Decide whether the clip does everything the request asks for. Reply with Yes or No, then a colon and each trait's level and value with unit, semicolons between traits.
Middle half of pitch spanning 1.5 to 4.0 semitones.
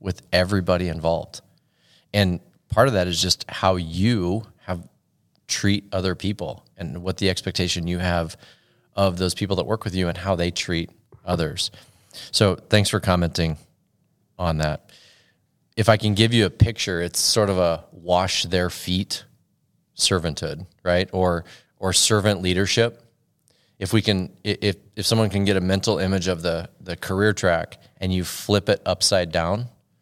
Yes: average, 2.7 semitones